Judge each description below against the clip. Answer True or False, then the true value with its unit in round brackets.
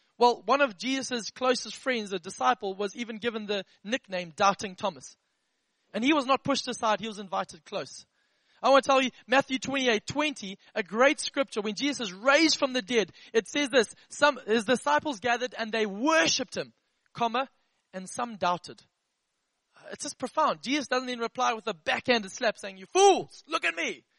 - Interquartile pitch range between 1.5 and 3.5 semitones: False (4.1 semitones)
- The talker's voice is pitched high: True (245 Hz)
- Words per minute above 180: True (190 wpm)